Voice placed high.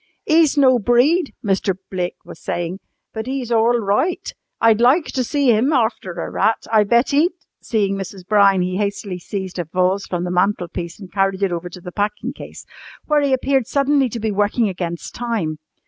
Yes: high, 210 Hz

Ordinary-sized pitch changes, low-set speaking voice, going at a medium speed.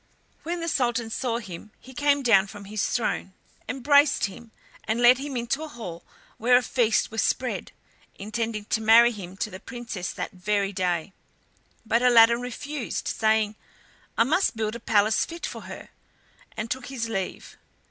No: average, 3.0 semitones; high, 230 Hz; average, 170 wpm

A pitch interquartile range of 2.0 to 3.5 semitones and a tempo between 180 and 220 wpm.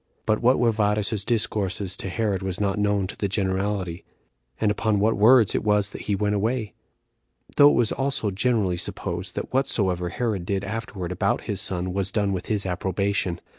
Yes: narrow, 2.4 semitones; average, 185 wpm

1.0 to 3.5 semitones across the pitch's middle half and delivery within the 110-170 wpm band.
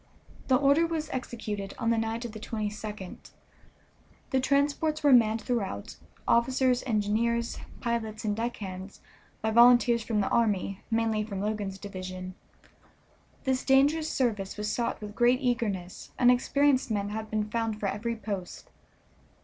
Yes: average, 3.1 semitones; average, 145 wpm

